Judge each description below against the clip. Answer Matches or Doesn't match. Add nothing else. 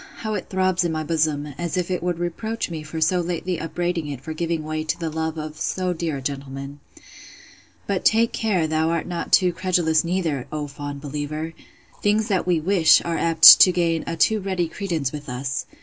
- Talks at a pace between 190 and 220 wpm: Matches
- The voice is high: Doesn't match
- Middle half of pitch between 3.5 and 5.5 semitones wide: Doesn't match